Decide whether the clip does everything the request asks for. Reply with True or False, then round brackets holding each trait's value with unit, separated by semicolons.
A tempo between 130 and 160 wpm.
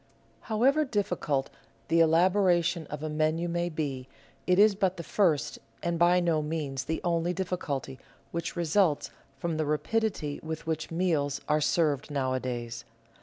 True (145 wpm)